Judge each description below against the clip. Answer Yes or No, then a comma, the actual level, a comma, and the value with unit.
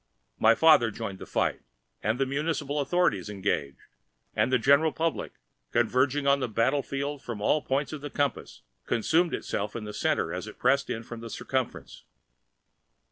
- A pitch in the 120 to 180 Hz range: Yes, low, 135 Hz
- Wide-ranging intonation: No, average, 4.3 semitones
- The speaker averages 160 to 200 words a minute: Yes, average, 165 wpm